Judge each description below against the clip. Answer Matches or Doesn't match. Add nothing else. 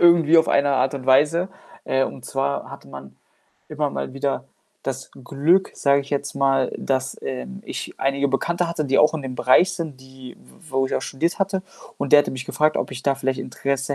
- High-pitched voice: Doesn't match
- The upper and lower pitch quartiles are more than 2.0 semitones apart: Matches